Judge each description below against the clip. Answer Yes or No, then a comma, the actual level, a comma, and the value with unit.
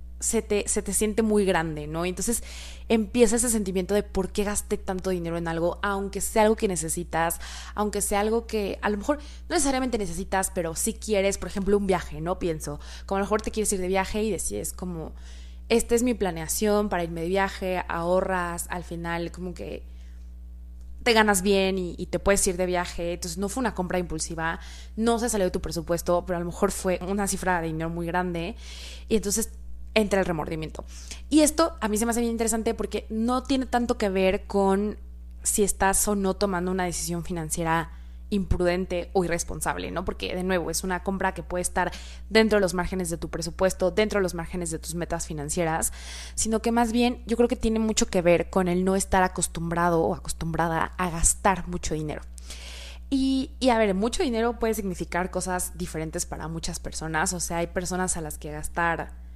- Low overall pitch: No, medium, 185 Hz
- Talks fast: Yes, fast, 205 wpm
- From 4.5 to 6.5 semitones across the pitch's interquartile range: No, average, 3.7 semitones